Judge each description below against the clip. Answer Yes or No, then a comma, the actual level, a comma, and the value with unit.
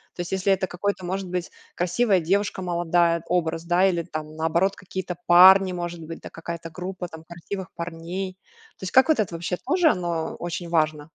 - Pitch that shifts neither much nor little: No, narrow, 2.1 semitones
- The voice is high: No, medium, 175 Hz